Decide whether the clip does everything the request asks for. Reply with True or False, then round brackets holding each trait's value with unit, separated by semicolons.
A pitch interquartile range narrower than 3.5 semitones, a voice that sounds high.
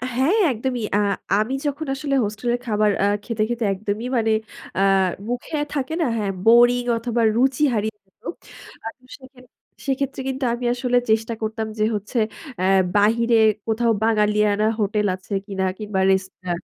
True (2.9 semitones; 225 Hz)